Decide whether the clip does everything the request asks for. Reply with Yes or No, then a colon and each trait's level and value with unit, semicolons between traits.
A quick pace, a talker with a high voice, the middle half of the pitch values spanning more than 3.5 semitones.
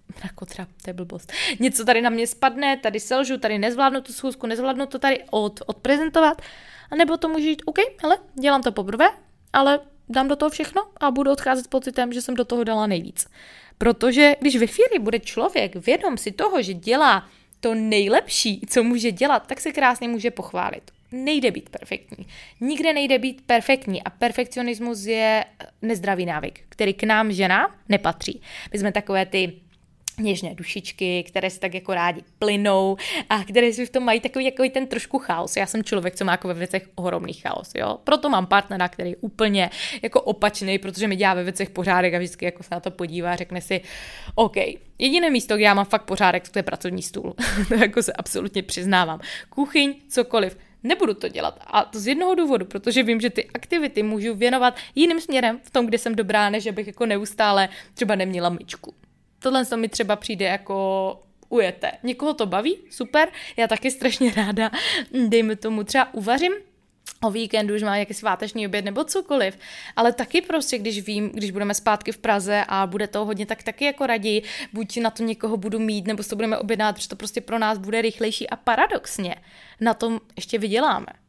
Yes: fast, 190 wpm; high, 225 Hz; average, 4.5 semitones